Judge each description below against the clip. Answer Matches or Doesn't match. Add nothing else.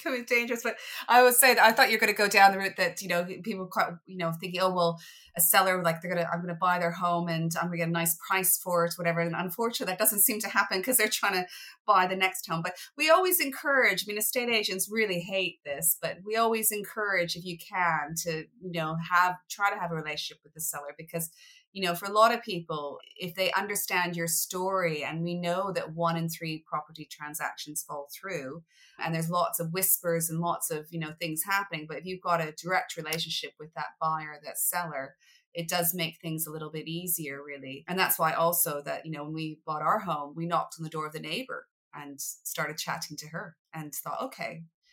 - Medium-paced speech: Doesn't match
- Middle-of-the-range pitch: Matches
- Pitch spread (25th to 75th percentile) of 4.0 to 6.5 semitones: Doesn't match